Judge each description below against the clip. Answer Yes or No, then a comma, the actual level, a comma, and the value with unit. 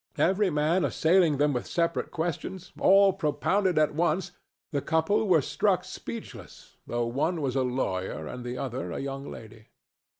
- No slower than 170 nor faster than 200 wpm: No, average, 160 wpm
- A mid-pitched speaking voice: Yes, medium, 155 Hz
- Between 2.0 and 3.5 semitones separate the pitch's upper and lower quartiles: No, wide, 5.4 semitones